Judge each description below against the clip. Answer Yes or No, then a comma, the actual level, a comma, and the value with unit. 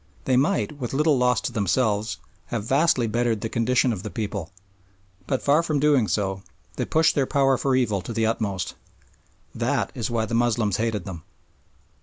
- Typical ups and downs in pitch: Yes, average, 4.0 semitones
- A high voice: No, low, 115 Hz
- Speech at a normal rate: Yes, average, 180 wpm